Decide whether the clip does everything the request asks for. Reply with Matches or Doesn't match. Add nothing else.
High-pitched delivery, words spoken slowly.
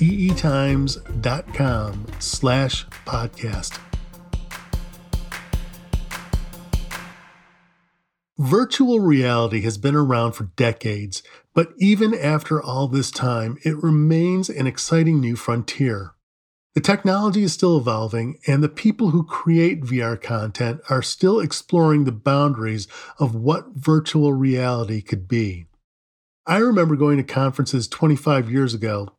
Doesn't match